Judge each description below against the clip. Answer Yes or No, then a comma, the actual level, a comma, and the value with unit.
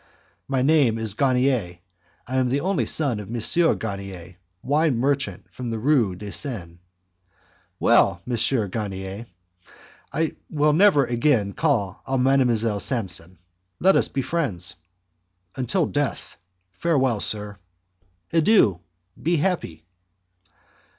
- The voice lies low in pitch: Yes, low, 125 Hz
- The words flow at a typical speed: No, slow, 115 wpm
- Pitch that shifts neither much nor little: No, wide, 5.9 semitones